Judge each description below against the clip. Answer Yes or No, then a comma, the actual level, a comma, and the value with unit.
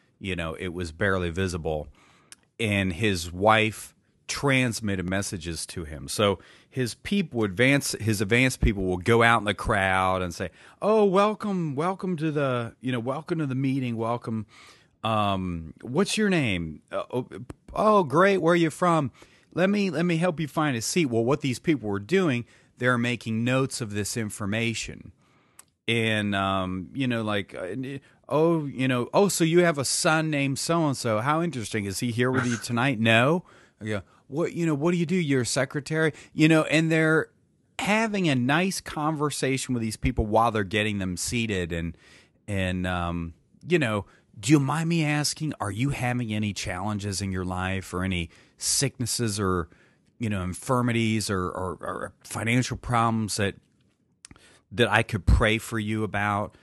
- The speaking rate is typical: Yes, average, 175 wpm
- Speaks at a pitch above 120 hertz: No, low, 115 Hz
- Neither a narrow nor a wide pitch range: No, wide, 6.7 semitones